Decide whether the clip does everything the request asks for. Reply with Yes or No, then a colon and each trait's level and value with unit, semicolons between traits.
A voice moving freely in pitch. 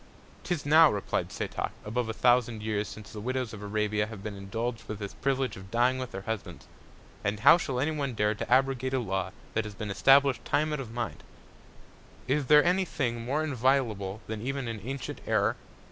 No: average, 4.2 semitones